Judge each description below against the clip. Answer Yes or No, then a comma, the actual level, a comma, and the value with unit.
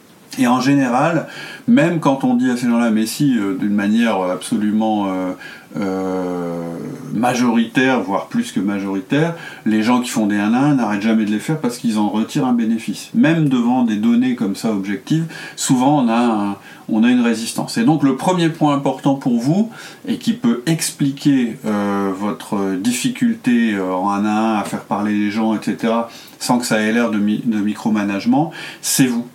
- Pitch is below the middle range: Yes, low, 120 Hz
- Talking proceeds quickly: No, average, 190 wpm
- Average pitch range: No, wide, 7.8 semitones